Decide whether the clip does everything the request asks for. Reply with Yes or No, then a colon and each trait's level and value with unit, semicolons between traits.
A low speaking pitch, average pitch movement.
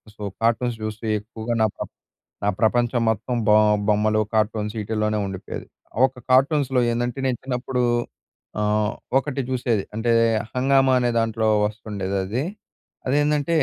Yes: low, 115 Hz; average, 3.1 semitones